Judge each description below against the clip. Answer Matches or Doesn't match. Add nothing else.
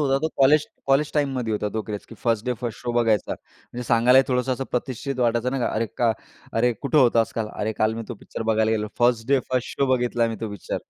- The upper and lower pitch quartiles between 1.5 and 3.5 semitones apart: Matches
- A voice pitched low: Matches